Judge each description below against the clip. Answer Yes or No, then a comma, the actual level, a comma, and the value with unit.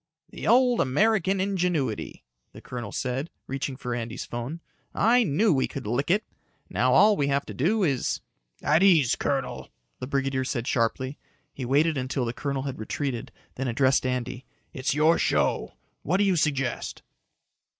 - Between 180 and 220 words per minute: No, average, 160 wpm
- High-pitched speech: No, medium, 140 Hz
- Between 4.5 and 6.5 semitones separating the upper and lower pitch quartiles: Yes, average, 5.0 semitones